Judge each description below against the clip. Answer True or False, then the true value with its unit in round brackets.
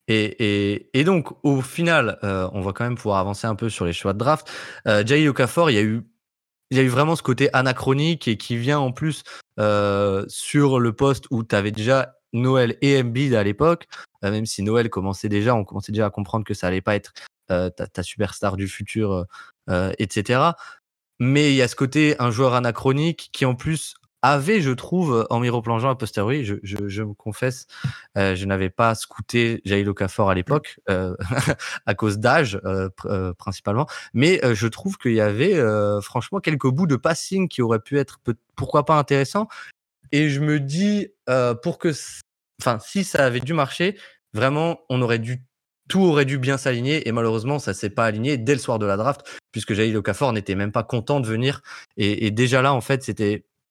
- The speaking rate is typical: True (210 wpm)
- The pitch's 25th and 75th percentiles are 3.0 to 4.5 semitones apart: False (5.4 semitones)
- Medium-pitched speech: False (120 Hz)